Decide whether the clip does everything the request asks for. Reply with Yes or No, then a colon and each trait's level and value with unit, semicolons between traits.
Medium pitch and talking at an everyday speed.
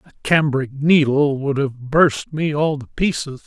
Yes: medium, 145 Hz; average, 175 wpm